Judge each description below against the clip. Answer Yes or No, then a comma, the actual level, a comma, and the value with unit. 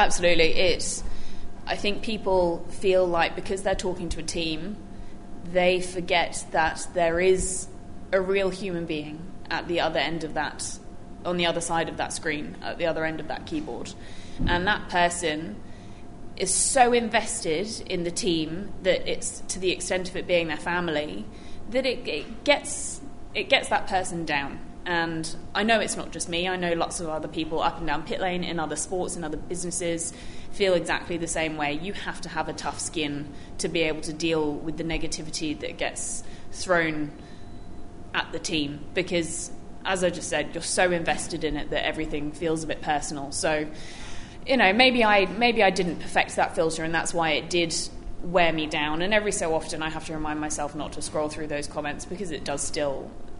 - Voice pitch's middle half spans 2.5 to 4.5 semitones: Yes, average, 2.8 semitones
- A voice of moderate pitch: Yes, medium, 165 Hz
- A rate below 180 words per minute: No, average, 195 wpm